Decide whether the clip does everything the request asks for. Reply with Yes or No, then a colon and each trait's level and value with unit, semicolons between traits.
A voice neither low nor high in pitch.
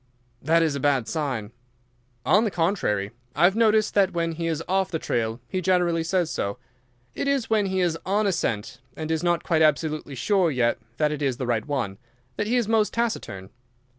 Yes: medium, 165 Hz